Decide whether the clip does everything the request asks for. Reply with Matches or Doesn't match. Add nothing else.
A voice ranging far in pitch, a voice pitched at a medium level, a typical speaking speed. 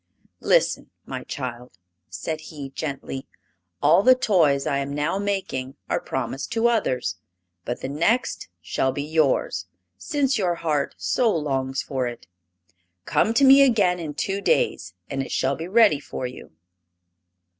Matches